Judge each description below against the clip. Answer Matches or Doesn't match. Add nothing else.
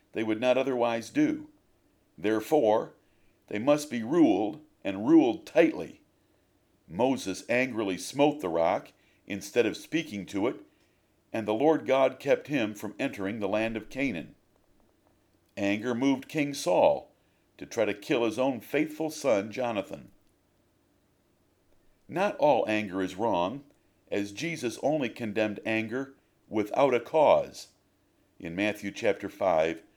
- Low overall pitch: Matches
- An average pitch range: Doesn't match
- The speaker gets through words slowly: Matches